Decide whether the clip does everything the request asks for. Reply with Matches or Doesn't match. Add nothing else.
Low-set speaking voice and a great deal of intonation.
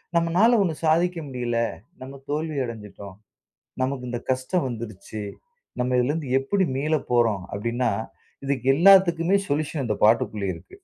Matches